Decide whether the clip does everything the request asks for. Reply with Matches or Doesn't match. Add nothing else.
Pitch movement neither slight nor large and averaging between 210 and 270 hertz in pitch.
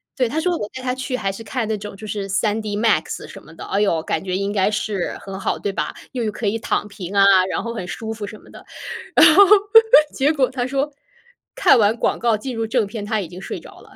Matches